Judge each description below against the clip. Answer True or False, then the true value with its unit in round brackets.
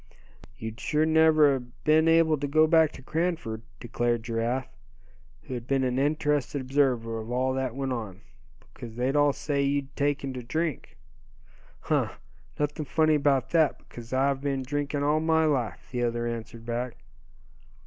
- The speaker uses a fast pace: False (160 wpm)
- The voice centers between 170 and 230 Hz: False (135 Hz)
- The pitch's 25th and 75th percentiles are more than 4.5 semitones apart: False (3.6 semitones)